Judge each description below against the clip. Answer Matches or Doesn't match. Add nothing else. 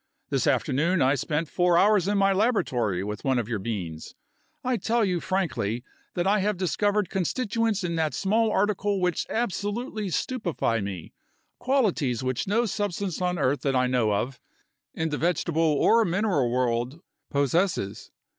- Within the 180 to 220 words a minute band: Doesn't match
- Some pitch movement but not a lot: Doesn't match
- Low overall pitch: Doesn't match